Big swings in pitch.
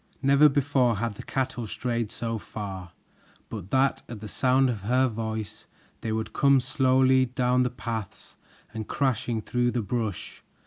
No: average, 3.0 semitones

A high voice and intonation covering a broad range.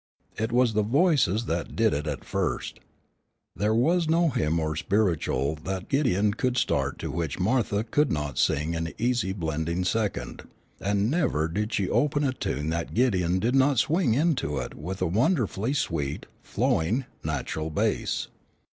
No: low, 100 Hz; wide, 7.5 semitones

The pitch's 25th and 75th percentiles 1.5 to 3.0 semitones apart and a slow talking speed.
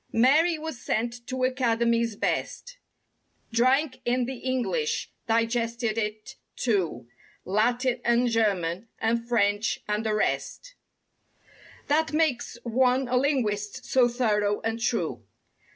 Yes: narrow, 2.6 semitones; slow, 105 wpm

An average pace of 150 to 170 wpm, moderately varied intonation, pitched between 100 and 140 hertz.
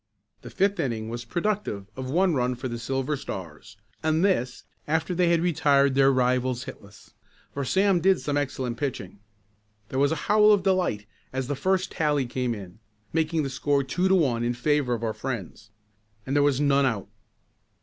No: average, 185 wpm; average, 4.9 semitones; low, 135 Hz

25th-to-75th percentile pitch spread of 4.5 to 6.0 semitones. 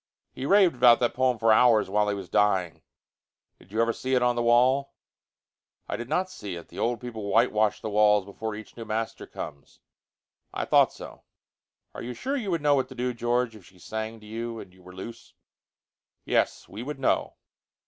No: average, 3.0 semitones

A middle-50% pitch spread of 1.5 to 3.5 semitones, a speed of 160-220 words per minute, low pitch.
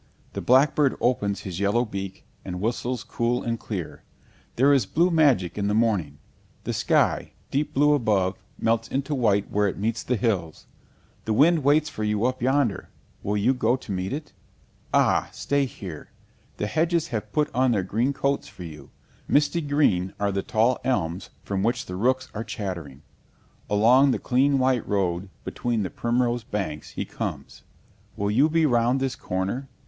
No: average, 5.0 semitones; average, 175 wpm; low, 115 Hz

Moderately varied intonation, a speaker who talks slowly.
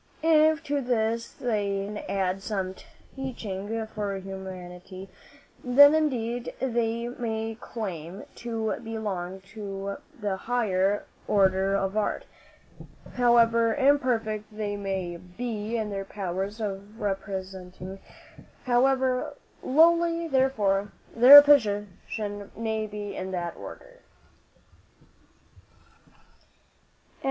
Yes: average, 3.8 semitones; slow, 95 wpm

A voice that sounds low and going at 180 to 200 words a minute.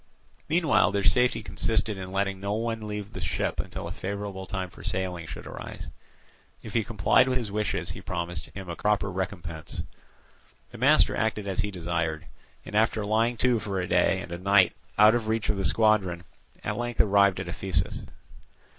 Yes: low, 100 Hz; average, 185 wpm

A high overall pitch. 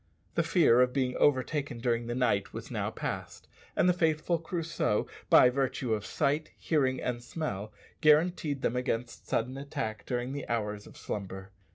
No: low, 130 Hz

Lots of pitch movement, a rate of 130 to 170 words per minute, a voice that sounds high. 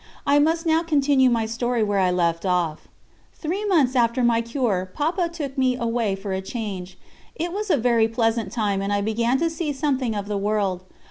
No: wide, 6.0 semitones; average, 200 wpm; high, 235 Hz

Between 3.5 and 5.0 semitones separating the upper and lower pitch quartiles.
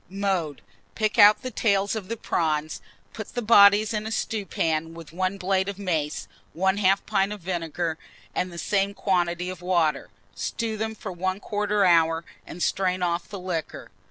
No: average, 3.1 semitones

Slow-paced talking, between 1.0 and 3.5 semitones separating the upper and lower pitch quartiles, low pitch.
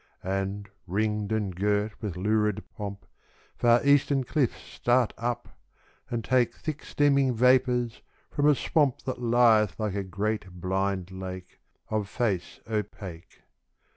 No: slow, 130 wpm; average, 3.9 semitones; low, 110 Hz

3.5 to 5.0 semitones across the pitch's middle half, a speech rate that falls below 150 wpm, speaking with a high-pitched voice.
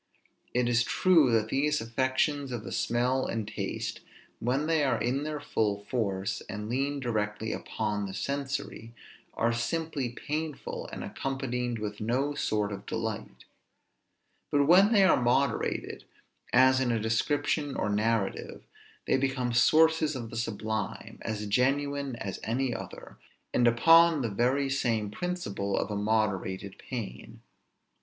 No: average, 4.3 semitones; average, 140 wpm; low, 120 Hz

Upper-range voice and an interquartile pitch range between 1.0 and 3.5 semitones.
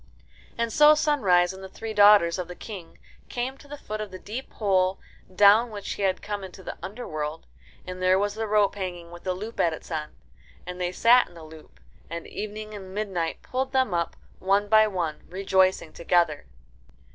Yes: high, 195 Hz; average, 3.2 semitones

